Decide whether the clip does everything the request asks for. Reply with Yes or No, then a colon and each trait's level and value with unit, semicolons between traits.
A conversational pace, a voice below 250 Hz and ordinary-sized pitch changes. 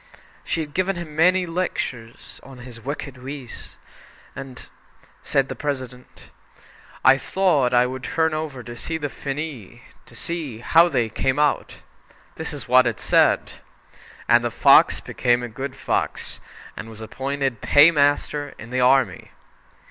Yes: average, 145 wpm; low, 135 Hz; average, 3.5 semitones